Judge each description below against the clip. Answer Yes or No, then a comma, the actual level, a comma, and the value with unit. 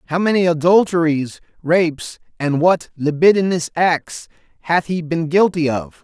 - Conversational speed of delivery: No, slow, 130 wpm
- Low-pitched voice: No, medium, 165 Hz